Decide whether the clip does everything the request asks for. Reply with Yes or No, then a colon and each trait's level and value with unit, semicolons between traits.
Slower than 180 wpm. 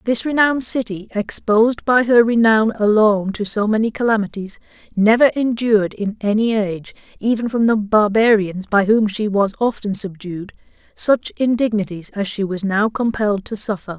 Yes: average, 155 wpm